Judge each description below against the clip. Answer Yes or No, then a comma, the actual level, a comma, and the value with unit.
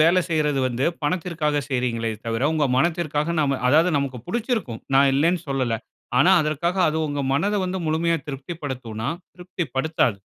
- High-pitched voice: No, medium, 150 Hz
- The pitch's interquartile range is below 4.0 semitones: No, average, 4.3 semitones